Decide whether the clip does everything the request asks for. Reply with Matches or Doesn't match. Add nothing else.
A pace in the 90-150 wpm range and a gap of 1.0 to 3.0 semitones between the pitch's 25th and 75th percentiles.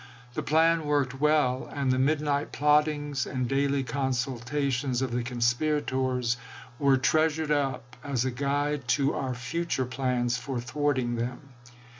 Matches